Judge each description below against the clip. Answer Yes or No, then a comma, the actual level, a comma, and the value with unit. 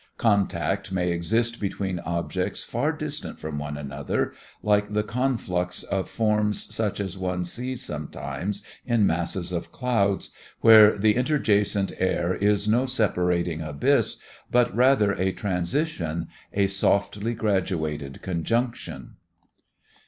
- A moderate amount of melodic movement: Yes, average, 4.5 semitones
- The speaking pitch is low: Yes, low, 100 Hz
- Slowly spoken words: Yes, slow, 120 wpm